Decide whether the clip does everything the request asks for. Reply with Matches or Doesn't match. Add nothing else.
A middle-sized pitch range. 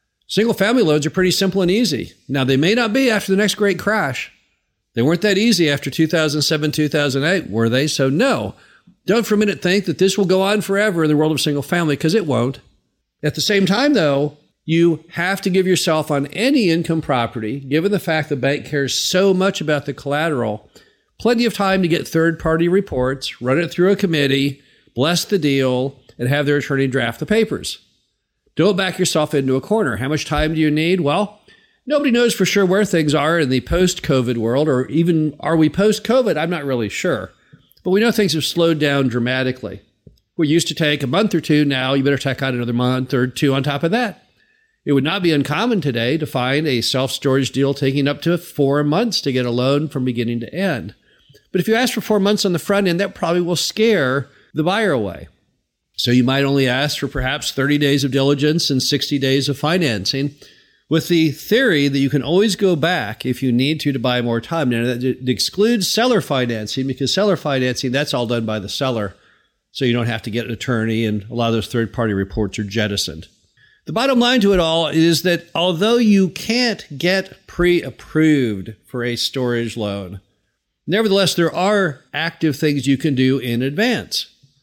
Doesn't match